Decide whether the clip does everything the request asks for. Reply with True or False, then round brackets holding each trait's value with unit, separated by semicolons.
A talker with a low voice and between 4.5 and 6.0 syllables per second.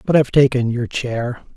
True (125 Hz; 5.1 syllables/s)